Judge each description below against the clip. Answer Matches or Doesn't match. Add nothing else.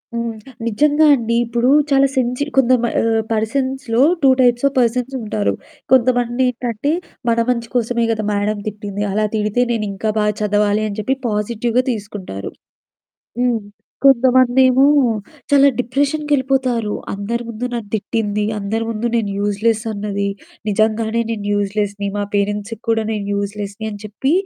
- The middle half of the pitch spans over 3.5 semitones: Doesn't match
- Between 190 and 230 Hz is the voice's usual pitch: Matches